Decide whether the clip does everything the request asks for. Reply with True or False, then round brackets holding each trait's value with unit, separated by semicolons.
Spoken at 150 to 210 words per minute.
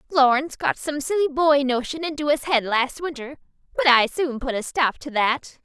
True (200 wpm)